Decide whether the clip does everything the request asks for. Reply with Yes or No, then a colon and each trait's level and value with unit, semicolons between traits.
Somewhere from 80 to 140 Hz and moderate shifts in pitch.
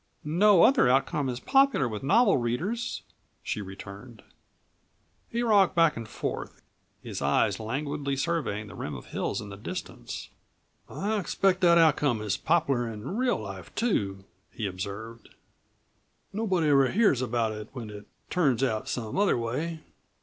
No: low, 135 Hz; wide, 8.6 semitones